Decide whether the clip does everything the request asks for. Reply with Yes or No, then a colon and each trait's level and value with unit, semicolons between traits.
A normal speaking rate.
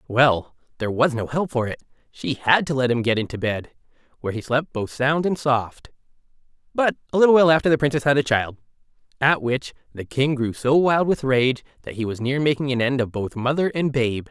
No: fast, 220 wpm